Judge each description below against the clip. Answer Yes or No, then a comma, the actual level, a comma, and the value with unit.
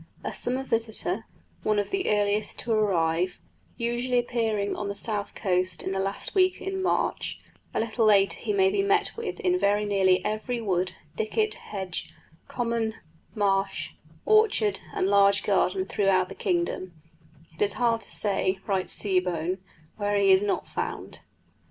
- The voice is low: No, high, 205 Hz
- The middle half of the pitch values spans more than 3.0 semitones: Yes, average, 3.7 semitones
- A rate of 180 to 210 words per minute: No, average, 160 wpm